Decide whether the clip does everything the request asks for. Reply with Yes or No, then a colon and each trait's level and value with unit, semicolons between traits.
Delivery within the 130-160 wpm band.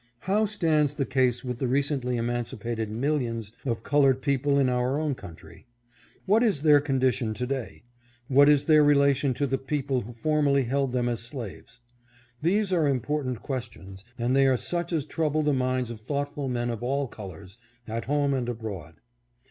No: average, 175 wpm